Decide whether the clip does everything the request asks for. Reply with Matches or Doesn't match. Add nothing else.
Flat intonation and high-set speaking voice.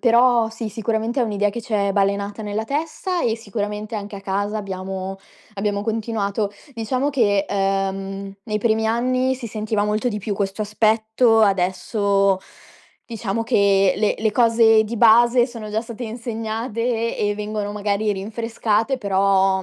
Matches